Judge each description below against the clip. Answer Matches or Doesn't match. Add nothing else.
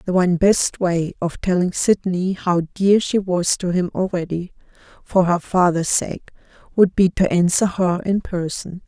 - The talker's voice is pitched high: Doesn't match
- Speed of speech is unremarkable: Matches